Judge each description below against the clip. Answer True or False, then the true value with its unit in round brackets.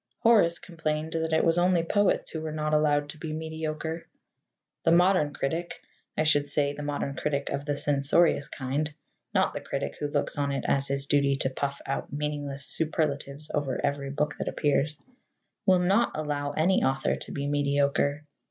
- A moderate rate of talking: True (180 wpm)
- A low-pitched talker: False (150 Hz)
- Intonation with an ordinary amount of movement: False (2.2 semitones)